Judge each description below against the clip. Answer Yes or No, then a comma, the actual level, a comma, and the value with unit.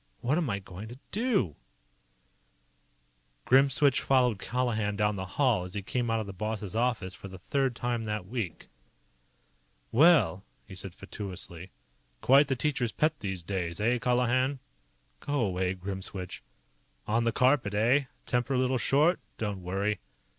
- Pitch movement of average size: Yes, average, 4.9 semitones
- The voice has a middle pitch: No, low, 110 Hz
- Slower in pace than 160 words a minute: Yes, average, 150 wpm